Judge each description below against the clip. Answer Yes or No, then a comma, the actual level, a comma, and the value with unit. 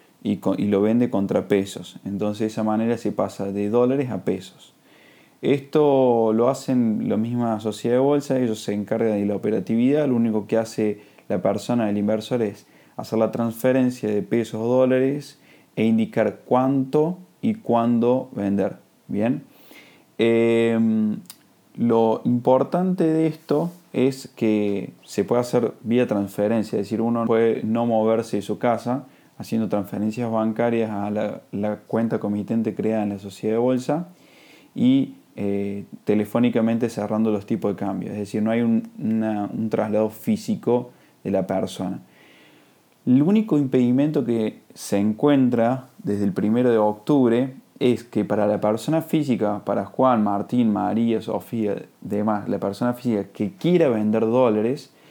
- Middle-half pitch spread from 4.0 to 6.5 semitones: No, average, 3.2 semitones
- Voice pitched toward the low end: Yes, low, 115 Hz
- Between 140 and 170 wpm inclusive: Yes, average, 150 wpm